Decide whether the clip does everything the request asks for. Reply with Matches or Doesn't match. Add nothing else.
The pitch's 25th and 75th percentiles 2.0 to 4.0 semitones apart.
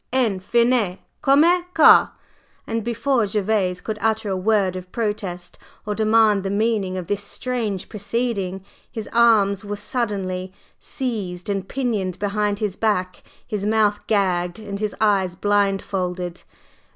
Matches